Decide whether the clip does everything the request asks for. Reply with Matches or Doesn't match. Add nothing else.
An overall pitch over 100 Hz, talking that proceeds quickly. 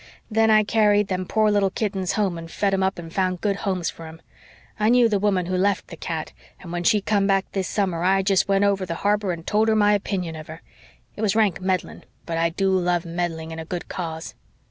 Matches